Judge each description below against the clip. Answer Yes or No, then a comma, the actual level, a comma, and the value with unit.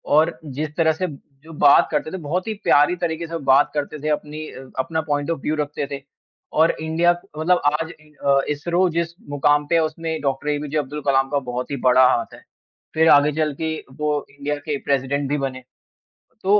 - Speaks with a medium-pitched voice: Yes, medium, 150 Hz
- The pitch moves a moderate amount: No, narrow, 2.2 semitones